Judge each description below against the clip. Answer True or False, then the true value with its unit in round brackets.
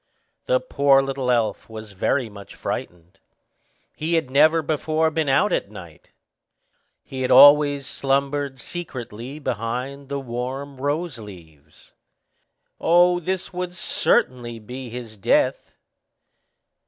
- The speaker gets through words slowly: True (115 wpm)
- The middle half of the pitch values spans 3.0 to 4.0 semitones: False (4.6 semitones)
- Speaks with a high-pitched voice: False (135 Hz)